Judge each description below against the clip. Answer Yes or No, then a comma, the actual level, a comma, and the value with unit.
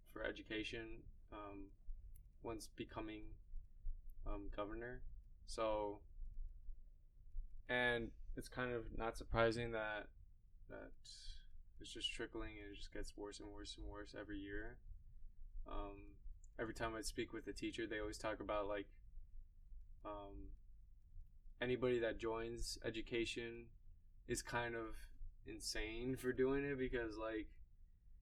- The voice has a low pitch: Yes, low, 105 Hz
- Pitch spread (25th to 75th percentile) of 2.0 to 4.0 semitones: No, average, 5.1 semitones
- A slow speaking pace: Yes, slow, 120 wpm